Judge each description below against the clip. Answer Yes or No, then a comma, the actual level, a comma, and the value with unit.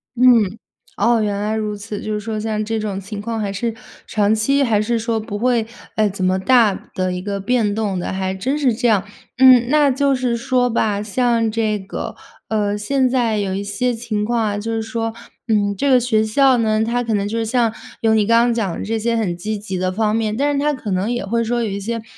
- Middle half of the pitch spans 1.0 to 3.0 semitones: Yes, narrow, 2.6 semitones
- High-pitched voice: Yes, high, 220 Hz